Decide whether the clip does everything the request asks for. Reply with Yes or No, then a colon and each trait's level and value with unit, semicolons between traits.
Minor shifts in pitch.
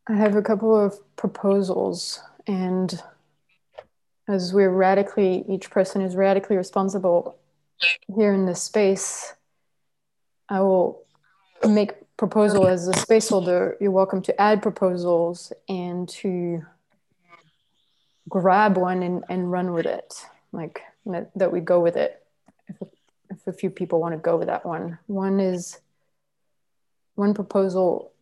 Yes: narrow, 2.0 semitones